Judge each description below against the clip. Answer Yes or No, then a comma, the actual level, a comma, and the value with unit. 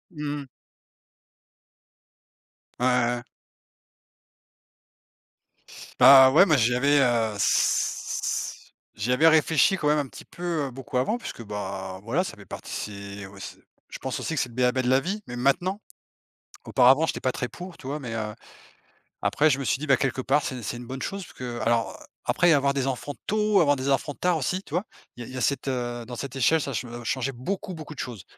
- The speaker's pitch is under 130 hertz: No, low, 135 Hz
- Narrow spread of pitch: No, average, 3.9 semitones